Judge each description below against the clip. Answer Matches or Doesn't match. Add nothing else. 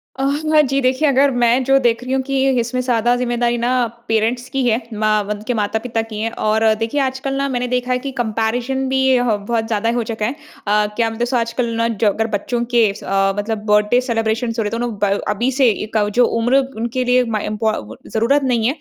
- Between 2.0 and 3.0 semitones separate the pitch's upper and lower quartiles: Matches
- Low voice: Doesn't match